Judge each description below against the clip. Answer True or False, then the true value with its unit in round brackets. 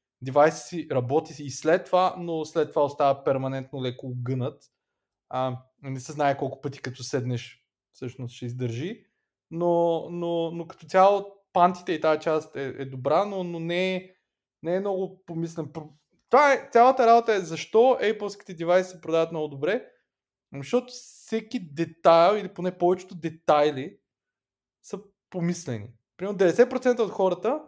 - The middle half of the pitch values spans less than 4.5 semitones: False (5.2 semitones)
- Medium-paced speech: True (150 wpm)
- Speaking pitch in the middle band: True (165 Hz)